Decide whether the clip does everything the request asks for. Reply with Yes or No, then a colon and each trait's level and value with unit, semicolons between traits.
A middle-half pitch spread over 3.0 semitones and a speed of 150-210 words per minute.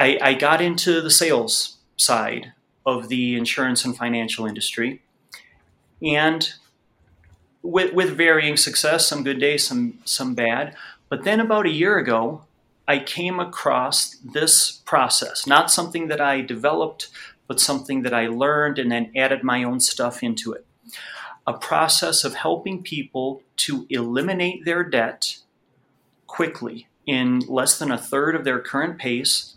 No: average, 4.5 semitones; average, 140 wpm